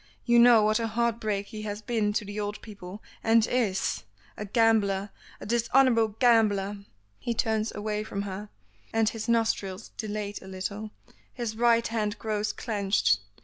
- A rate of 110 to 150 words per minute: No, average, 160 wpm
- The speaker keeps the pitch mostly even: Yes, narrow, 1.9 semitones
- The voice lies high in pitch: Yes, high, 215 Hz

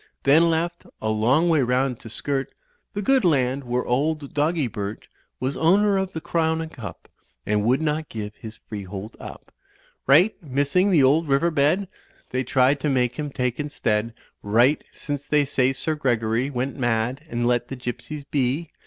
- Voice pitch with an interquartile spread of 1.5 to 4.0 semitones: No, average, 4.4 semitones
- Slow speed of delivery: No, average, 185 wpm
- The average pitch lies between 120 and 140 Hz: Yes, low, 135 Hz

